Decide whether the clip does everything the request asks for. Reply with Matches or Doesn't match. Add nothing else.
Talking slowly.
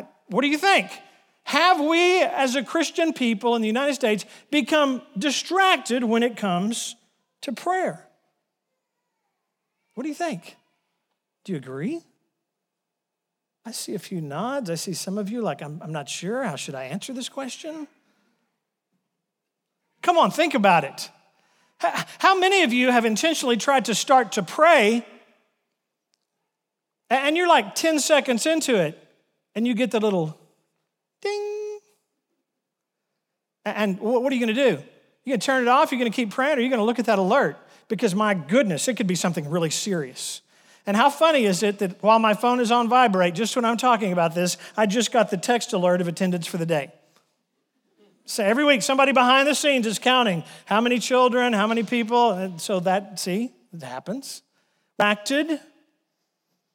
Doesn't match